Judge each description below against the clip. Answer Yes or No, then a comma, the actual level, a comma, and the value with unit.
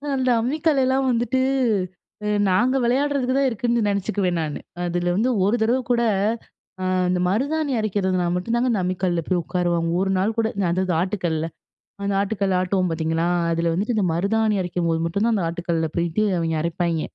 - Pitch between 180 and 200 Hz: Yes, high, 190 Hz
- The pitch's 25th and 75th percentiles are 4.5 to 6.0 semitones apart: Yes, average, 5.3 semitones